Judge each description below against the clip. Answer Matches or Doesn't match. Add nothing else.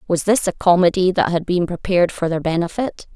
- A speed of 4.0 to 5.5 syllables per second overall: Doesn't match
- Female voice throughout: Matches